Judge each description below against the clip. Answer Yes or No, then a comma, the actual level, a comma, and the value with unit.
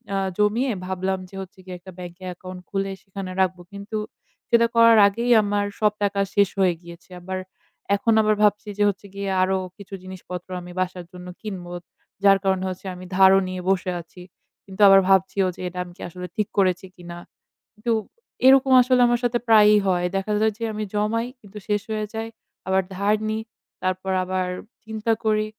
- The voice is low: No, high, 195 Hz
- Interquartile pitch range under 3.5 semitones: Yes, narrow, 2.4 semitones